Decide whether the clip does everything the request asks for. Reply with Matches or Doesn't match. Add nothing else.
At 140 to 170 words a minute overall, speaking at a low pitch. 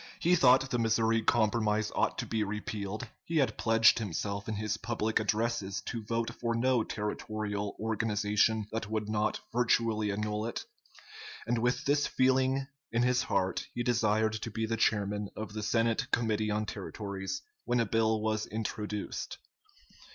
Matches